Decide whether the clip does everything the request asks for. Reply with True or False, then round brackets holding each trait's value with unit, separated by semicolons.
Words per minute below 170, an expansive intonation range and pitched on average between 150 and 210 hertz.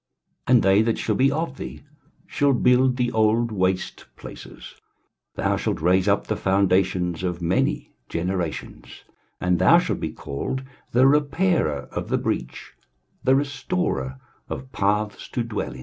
False (150 wpm; 6.2 semitones; 105 Hz)